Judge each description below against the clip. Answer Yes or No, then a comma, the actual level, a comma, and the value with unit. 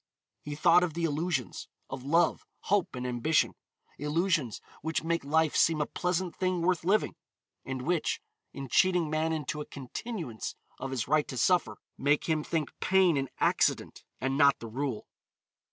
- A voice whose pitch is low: No, medium, 155 Hz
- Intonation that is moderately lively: Yes, average, 4.2 semitones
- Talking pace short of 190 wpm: Yes, average, 165 wpm